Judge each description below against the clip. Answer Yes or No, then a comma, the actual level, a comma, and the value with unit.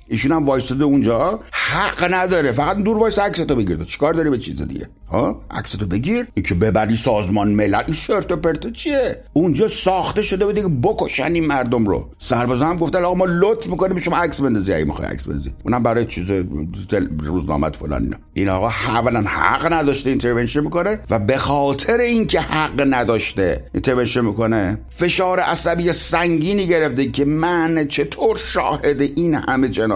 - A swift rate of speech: Yes, fast, 165 wpm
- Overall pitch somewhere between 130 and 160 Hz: Yes, medium, 140 Hz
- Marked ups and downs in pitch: Yes, wide, 7.8 semitones